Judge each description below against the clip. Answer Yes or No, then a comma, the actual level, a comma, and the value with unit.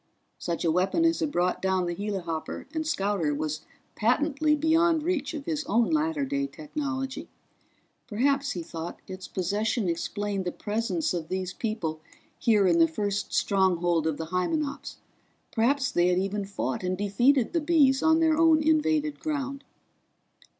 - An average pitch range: No, wide, 8.4 semitones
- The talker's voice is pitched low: No, high, 220 Hz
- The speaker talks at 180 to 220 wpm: No, average, 155 wpm